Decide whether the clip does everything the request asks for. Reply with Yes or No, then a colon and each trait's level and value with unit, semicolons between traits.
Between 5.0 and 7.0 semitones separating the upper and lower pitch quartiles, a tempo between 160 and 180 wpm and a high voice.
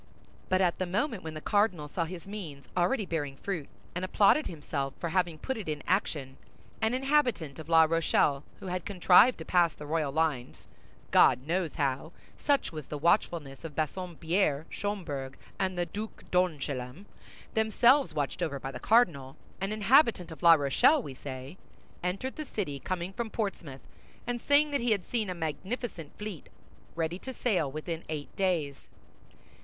No: wide, 5.5 semitones; average, 165 wpm; medium, 175 Hz